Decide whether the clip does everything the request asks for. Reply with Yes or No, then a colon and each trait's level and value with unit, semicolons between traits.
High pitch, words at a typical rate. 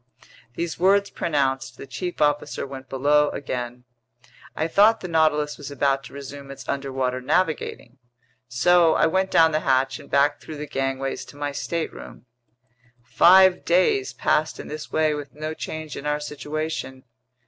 No: medium, 145 Hz; average, 160 wpm